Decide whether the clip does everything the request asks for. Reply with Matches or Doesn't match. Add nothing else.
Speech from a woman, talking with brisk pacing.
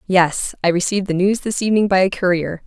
Matches